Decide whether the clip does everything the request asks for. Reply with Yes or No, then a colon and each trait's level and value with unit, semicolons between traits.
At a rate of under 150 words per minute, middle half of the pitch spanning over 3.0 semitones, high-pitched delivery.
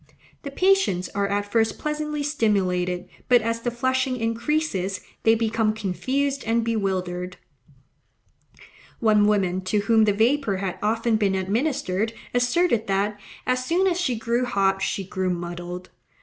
Yes: average, 140 wpm; average, 4.7 semitones; high, 220 Hz